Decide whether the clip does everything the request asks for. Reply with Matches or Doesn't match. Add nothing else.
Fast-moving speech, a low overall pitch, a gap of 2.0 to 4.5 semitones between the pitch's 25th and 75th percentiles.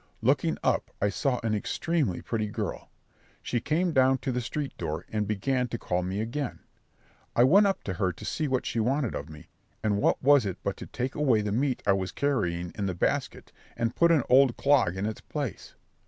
Doesn't match